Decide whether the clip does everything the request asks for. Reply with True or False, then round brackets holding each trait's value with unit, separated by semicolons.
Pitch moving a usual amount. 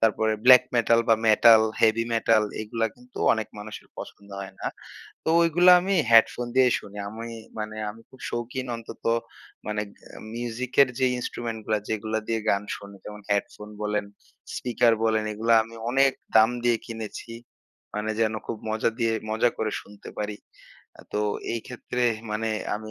False (1.8 semitones)